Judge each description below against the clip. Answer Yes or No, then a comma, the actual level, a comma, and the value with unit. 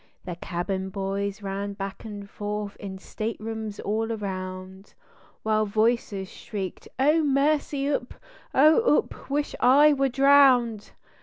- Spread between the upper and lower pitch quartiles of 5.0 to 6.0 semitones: Yes, average, 5.3 semitones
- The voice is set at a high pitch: Yes, high, 215 Hz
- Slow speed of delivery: Yes, slow, 125 wpm